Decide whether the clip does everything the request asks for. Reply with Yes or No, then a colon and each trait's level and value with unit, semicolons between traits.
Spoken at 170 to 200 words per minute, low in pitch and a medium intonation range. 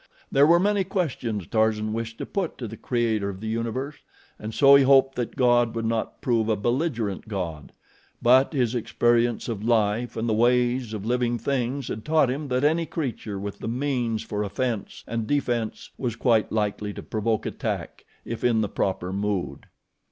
Yes: average, 180 wpm; low, 115 Hz; average, 3.0 semitones